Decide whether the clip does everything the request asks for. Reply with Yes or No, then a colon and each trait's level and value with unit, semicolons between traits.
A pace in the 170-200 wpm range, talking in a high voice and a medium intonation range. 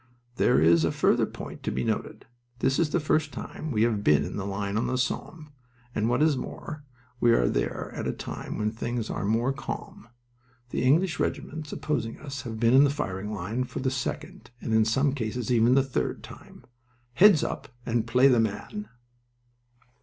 No: average, 195 wpm; low, 125 Hz; average, 4.7 semitones